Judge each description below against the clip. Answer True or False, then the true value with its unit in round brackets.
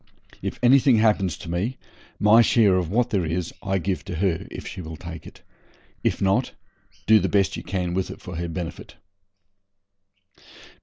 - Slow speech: False (175 wpm)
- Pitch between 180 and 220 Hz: False (95 Hz)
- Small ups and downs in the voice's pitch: False (3.6 semitones)